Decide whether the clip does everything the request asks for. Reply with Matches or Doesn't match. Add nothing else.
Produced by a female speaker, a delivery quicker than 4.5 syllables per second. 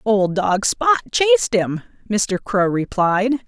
Doesn't match